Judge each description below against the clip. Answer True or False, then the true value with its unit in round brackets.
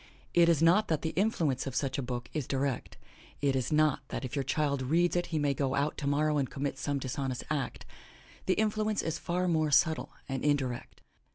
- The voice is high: False (145 Hz)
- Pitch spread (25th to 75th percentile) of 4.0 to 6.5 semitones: False (3.4 semitones)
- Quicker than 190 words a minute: True (205 wpm)